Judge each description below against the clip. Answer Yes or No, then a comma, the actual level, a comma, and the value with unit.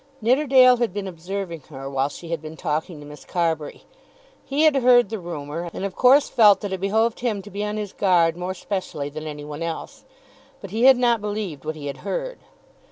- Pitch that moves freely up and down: Yes, wide, 6.2 semitones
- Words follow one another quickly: Yes, fast, 215 wpm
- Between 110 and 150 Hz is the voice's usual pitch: No, high, 190 Hz